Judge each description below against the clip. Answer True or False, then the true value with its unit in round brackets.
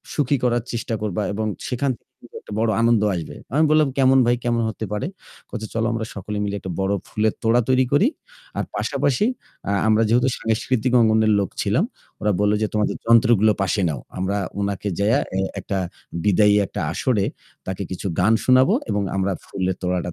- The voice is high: False (110 Hz)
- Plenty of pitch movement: False (3.0 semitones)